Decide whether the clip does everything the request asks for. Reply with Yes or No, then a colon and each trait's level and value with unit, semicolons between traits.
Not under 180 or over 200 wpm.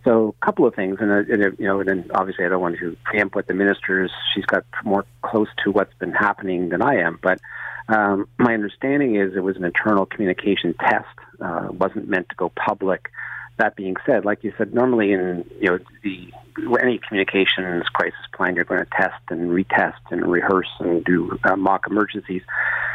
Yes: average, 195 wpm